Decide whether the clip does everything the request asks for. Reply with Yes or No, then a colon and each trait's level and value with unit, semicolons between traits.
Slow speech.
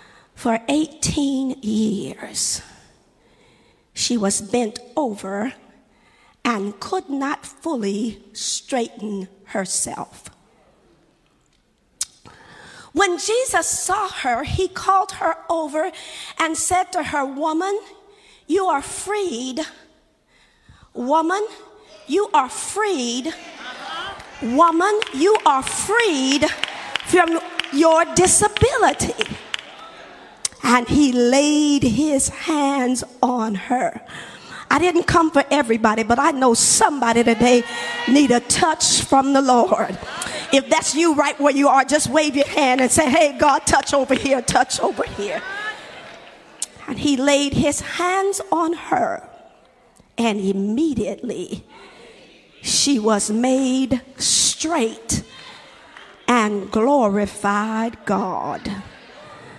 Yes: slow, 100 wpm